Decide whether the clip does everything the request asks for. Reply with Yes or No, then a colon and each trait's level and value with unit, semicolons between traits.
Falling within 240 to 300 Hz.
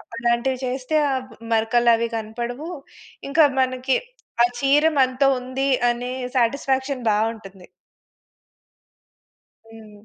Yes: very high, 250 Hz